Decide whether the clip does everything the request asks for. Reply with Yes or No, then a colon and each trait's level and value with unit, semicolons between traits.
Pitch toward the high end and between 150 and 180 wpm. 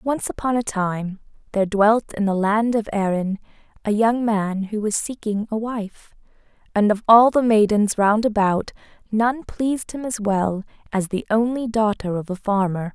Yes: high, 215 Hz; average, 175 wpm